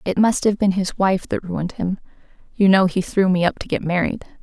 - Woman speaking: Yes, female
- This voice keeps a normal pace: No, fast, 245 wpm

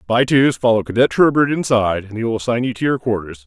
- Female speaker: No, male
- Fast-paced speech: Yes, fast, 225 wpm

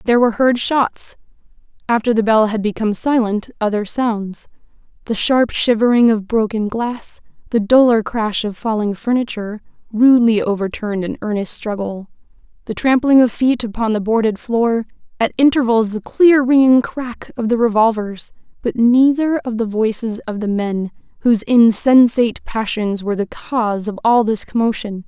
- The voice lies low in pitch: No, high, 225 Hz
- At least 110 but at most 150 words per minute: Yes, average, 145 wpm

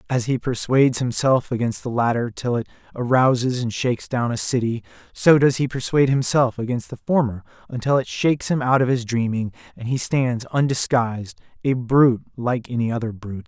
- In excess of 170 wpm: Yes, average, 185 wpm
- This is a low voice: Yes, low, 125 Hz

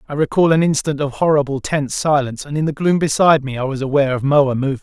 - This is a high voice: No, medium, 145 Hz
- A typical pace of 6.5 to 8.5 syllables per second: Yes, 6.9 syllables/s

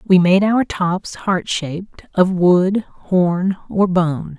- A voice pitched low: No, medium, 185 Hz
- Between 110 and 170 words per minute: Yes, average, 150 wpm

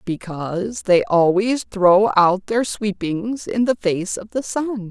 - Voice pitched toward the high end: Yes, high, 205 Hz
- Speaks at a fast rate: No, average, 160 wpm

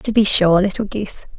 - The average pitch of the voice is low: No, high, 200 Hz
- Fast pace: Yes, fast, 215 wpm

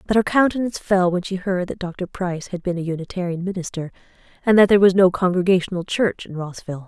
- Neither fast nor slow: No, fast, 210 wpm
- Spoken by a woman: Yes, female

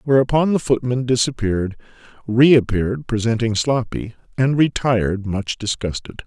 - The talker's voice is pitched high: No, low, 120 Hz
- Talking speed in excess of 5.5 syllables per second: No, 4.8 syllables/s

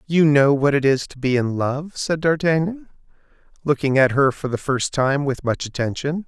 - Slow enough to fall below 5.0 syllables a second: Yes, 4.8 syllables/s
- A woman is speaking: No, male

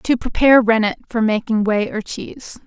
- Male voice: No, female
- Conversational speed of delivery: Yes, average, 180 wpm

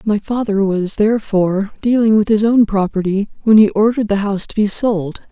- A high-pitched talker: Yes, high, 210 Hz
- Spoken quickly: No, average, 190 wpm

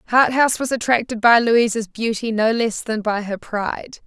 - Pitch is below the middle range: No, high, 230 Hz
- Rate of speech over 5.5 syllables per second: No, 5.0 syllables/s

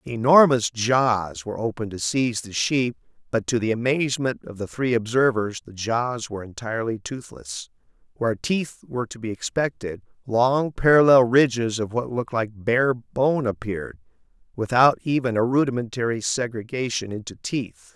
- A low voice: Yes, low, 120 Hz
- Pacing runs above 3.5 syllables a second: Yes, 5.0 syllables/s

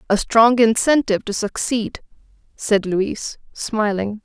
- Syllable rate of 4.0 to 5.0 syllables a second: Yes, 4.1 syllables/s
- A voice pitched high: Yes, high, 215 Hz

